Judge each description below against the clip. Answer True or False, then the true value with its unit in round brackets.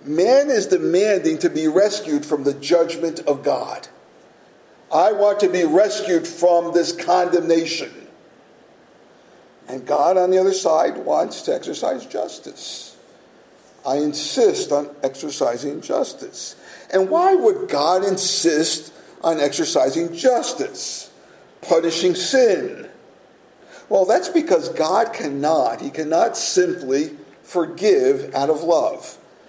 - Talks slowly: True (115 wpm)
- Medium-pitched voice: True (180 Hz)